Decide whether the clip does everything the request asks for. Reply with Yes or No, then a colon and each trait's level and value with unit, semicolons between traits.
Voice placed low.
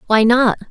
No: high, 230 Hz